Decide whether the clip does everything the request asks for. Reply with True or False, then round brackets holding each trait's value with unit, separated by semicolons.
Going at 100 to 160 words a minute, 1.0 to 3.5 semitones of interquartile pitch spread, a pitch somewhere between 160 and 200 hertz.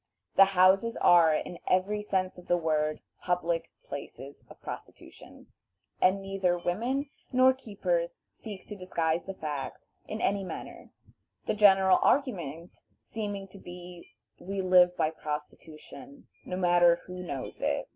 True (135 wpm; 2.9 semitones; 185 Hz)